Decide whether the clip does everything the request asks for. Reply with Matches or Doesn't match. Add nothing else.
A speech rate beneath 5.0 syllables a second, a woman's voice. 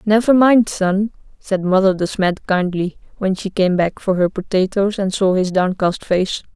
Matches